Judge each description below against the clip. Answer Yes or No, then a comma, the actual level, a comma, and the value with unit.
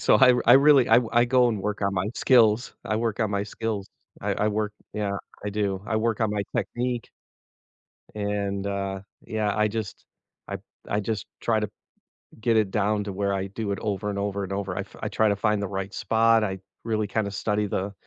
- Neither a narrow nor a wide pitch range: No, narrow, 2.0 semitones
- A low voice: Yes, low, 105 Hz